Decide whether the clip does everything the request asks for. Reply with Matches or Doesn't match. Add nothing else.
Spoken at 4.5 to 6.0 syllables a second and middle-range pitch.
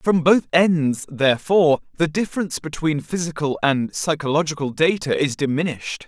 Matches